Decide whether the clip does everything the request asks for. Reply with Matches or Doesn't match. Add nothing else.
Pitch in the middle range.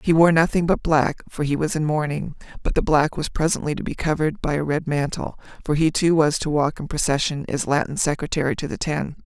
Matches